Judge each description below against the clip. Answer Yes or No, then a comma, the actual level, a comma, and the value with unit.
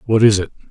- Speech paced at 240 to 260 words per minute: Yes, fast, 255 wpm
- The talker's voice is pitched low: Yes, low, 105 Hz